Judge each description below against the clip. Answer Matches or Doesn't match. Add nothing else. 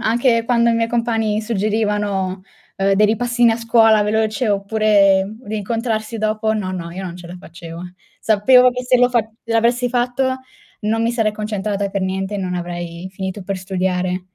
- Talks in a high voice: Matches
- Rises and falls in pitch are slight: Doesn't match